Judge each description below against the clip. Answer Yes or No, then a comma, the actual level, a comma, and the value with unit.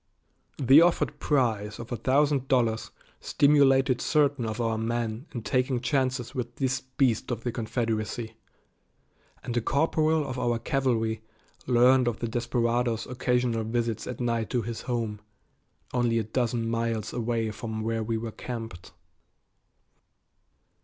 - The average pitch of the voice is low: Yes, low, 120 Hz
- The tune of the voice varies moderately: No, narrow, 2.3 semitones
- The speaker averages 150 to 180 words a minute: No, average, 140 wpm